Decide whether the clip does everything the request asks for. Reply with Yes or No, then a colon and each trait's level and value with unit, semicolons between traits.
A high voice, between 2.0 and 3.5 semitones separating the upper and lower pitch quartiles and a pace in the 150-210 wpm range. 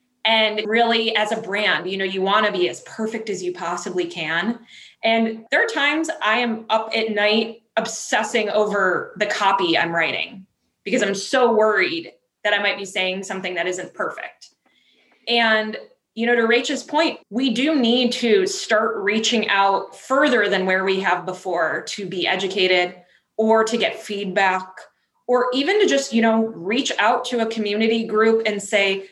Yes: high, 220 Hz; average, 3.1 semitones; average, 175 wpm